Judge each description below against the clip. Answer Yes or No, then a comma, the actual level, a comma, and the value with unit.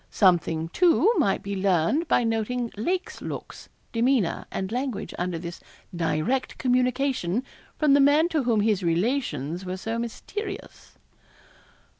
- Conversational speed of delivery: No, slow, 130 wpm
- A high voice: Yes, high, 230 Hz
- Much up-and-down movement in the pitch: Yes, wide, 7.0 semitones